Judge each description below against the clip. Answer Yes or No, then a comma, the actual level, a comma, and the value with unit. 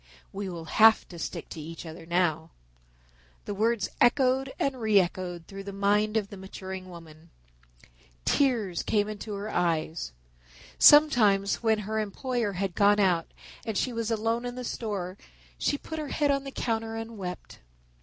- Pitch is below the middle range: No, high, 205 Hz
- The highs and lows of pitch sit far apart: No, average, 3.9 semitones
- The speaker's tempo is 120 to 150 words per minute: No, average, 165 wpm